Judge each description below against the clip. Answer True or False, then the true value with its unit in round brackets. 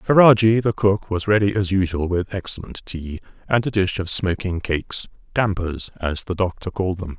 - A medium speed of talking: True (185 wpm)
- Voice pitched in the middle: False (95 Hz)